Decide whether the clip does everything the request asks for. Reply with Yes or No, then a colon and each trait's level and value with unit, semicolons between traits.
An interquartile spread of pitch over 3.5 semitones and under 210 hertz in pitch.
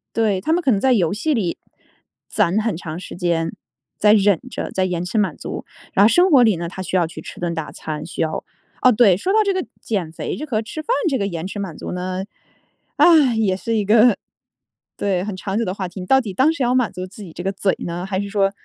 Yes: average, 4.2 semitones; high, 200 Hz